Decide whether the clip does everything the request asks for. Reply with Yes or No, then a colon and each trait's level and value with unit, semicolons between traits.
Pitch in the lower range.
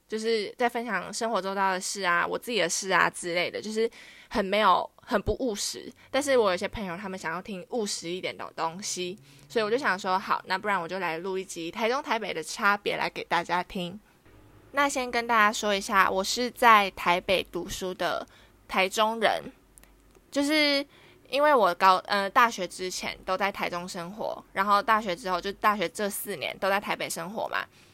No: high, 195 Hz